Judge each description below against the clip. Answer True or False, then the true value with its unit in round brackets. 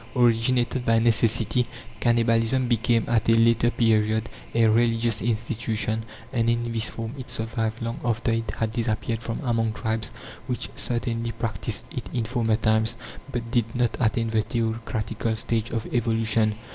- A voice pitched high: False (115 Hz)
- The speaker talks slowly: False (150 wpm)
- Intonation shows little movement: True (0.9 semitones)